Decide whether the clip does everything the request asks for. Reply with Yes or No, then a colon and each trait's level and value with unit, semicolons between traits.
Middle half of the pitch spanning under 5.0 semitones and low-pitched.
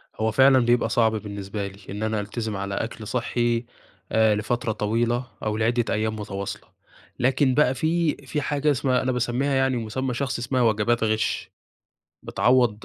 Yes: average, 3.0 semitones; low, 120 Hz